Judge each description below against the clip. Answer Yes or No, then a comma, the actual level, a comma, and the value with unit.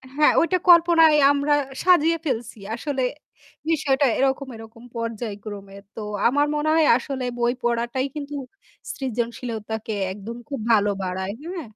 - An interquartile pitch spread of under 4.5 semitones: No, average, 4.8 semitones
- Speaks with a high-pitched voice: Yes, very high, 250 Hz